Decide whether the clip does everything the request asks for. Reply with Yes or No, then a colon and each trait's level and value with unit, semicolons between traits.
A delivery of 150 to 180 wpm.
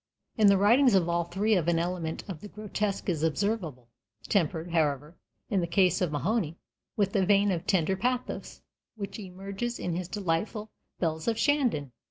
Yes: average, 170 wpm